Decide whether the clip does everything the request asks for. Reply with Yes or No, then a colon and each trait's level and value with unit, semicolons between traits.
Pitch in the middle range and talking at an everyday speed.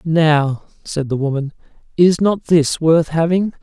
Yes: medium, 160 Hz; average, 150 wpm